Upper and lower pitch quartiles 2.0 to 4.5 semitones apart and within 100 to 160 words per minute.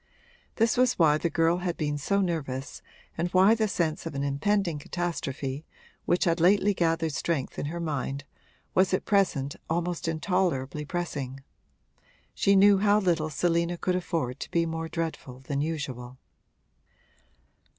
Yes: average, 4.0 semitones; average, 150 wpm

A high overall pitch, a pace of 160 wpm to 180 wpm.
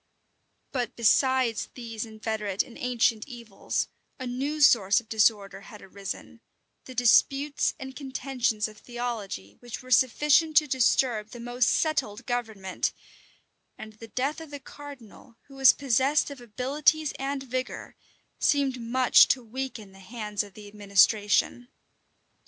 No: high, 245 Hz; slow, 135 wpm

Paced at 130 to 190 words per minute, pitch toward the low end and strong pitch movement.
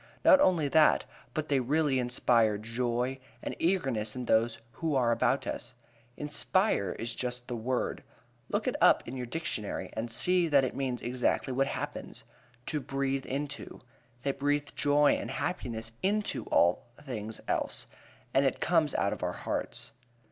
No: average, 160 wpm; low, 130 Hz; average, 3.7 semitones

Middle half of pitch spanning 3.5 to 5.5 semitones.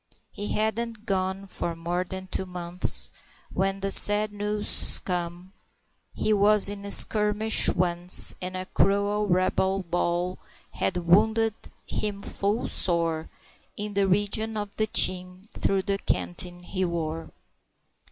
No: narrow, 2.5 semitones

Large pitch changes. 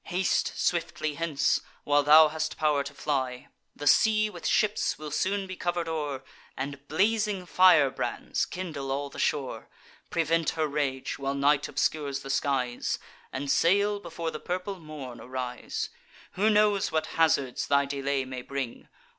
No: average, 4.1 semitones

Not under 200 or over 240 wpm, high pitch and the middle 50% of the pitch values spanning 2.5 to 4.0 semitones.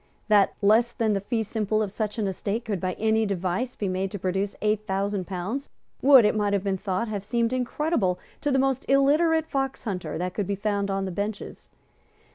Yes: fast, 205 wpm; high, 210 Hz; average, 3.4 semitones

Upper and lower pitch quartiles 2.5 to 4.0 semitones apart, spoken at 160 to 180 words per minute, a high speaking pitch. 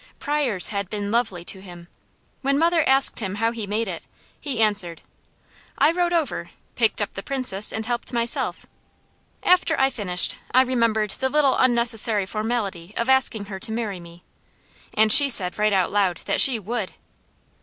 No: average, 4.6 semitones; average, 170 wpm; high, 220 Hz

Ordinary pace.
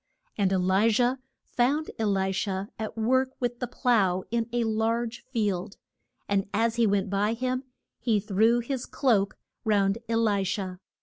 Yes: average, 170 wpm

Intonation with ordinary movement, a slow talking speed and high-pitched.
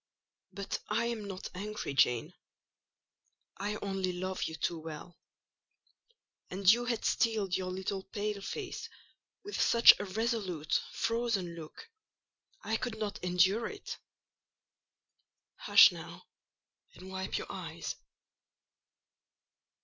Yes: average, 3.5 semitones; slow, 110 wpm; high, 200 Hz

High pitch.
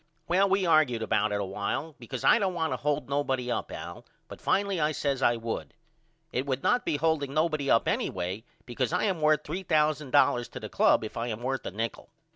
No: medium, 140 Hz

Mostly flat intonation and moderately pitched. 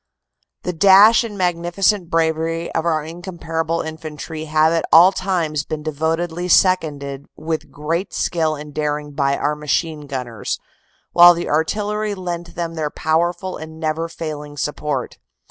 Yes: narrow, 2.3 semitones; medium, 160 Hz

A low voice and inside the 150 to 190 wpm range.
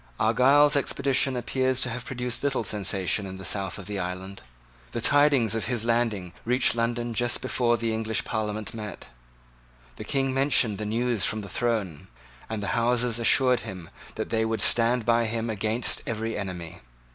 Yes: low, 115 Hz; average, 170 wpm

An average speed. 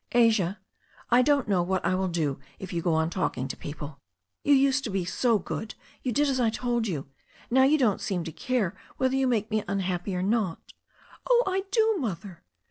No: fast, 215 wpm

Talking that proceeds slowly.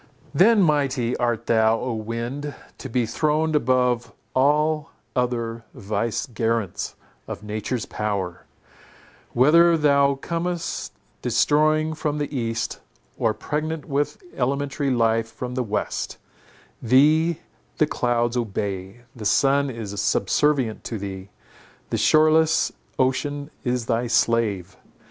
Yes: slow, 110 wpm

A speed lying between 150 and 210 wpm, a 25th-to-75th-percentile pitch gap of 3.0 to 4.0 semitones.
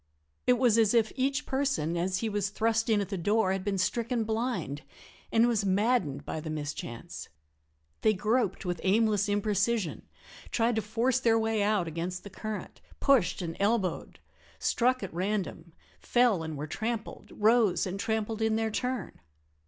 Yes: average, 165 wpm; average, 3.6 semitones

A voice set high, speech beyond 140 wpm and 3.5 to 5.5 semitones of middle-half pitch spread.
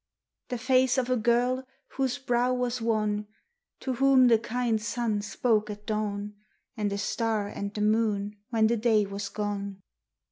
No: high, 225 Hz; average, 165 wpm; average, 3.0 semitones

